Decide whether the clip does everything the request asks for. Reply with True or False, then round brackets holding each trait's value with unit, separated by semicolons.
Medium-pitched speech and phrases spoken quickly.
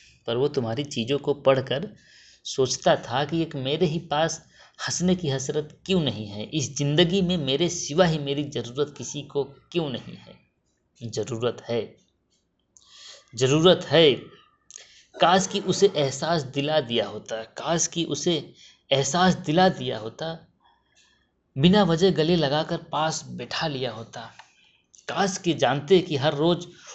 False (150 Hz; 145 wpm)